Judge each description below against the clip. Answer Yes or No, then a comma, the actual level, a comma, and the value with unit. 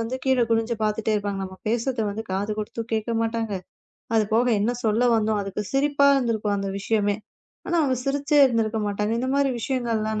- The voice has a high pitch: Yes, high, 225 Hz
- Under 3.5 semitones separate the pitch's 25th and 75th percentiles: Yes, average, 2.8 semitones